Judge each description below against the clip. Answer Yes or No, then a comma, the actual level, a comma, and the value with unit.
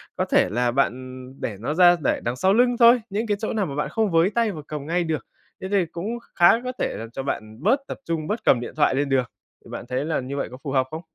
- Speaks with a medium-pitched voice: Yes, medium, 160 Hz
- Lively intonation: Yes, wide, 7.7 semitones